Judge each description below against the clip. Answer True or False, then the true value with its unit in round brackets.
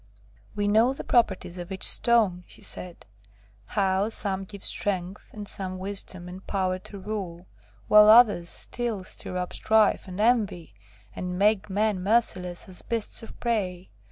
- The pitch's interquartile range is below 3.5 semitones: True (2.8 semitones)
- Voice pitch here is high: True (195 Hz)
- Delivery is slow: False (155 wpm)